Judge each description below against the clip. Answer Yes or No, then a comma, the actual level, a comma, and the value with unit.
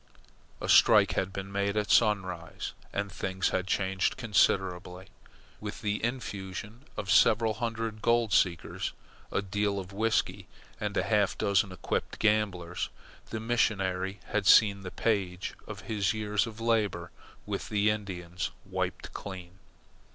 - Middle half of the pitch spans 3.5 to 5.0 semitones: No, narrow, 2.4 semitones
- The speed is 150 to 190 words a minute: No, slow, 135 wpm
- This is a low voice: Yes, low, 100 Hz